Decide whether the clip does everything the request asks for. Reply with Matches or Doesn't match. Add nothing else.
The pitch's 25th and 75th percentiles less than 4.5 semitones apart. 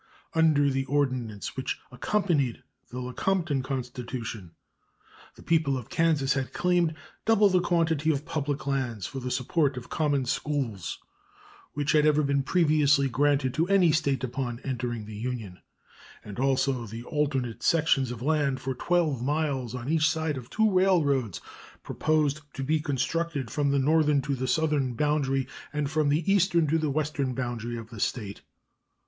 Matches